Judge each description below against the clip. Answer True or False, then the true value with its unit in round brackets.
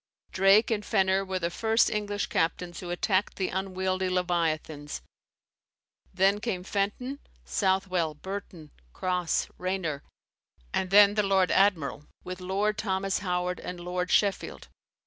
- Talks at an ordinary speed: False (125 wpm)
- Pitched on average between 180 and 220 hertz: True (190 Hz)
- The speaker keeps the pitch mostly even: True (1.9 semitones)